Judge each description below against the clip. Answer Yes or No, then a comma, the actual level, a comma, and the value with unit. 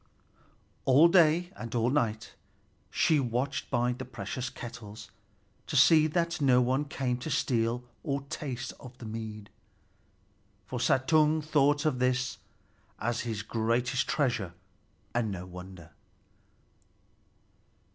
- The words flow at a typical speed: No, slow, 120 wpm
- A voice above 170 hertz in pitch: No, low, 125 Hz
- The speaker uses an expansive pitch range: No, average, 4.1 semitones